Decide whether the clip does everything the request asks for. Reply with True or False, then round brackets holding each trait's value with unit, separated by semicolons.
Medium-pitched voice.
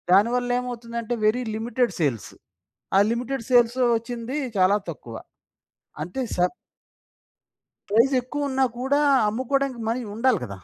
False (240 Hz)